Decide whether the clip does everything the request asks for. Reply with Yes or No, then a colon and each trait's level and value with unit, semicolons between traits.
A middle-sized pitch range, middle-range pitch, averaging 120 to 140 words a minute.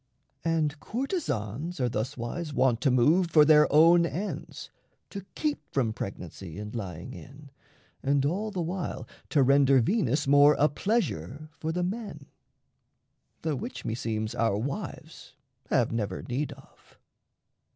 No: wide, 5.9 semitones; medium, 145 Hz; slow, 135 wpm